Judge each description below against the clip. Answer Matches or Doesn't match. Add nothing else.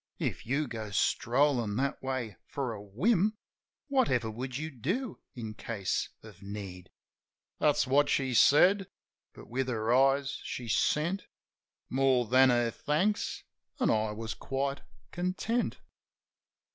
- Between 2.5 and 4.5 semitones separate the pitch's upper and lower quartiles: Doesn't match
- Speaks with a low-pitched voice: Matches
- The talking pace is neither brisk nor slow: Doesn't match